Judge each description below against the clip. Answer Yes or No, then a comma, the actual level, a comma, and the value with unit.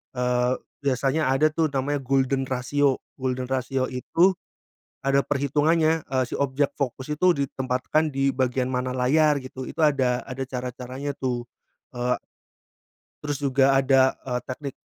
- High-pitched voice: No, low, 135 Hz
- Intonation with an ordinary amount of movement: No, narrow, 2.0 semitones